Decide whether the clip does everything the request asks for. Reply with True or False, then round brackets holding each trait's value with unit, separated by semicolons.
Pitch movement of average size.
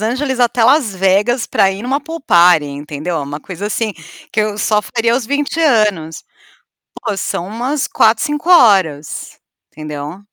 False (6.0 semitones)